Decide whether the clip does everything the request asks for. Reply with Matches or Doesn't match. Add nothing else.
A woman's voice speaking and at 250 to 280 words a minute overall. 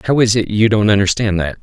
Doesn't match